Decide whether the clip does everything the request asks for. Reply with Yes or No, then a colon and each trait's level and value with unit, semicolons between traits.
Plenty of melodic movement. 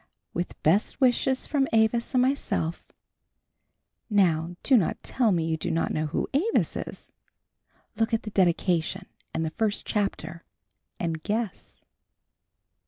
Yes: wide, 6.2 semitones